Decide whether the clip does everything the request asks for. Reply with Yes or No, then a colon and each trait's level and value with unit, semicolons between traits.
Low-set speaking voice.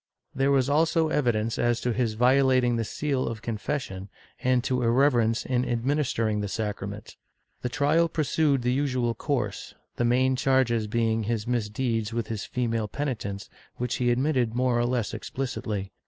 Yes: low, 120 Hz